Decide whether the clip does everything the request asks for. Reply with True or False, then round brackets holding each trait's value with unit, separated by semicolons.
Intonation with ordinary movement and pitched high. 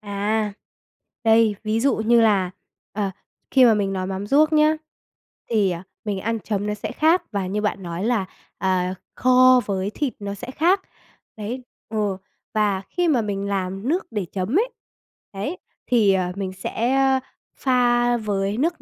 True (4.1 semitones; 215 Hz)